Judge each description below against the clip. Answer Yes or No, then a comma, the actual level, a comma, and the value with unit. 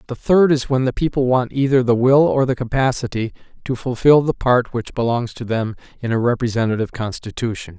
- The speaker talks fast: No, average, 195 wpm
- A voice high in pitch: No, low, 125 Hz